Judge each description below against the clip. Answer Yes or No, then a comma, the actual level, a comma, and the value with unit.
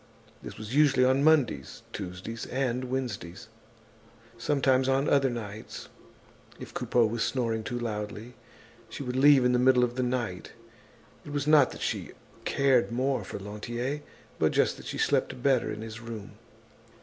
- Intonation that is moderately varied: Yes, average, 3.0 semitones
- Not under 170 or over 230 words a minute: No, average, 160 wpm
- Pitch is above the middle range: No, low, 125 Hz